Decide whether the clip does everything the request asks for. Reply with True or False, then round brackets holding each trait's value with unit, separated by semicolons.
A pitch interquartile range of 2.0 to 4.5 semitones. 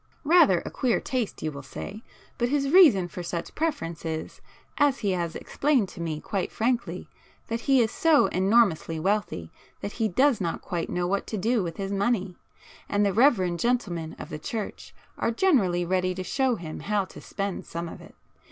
False (5.6 semitones)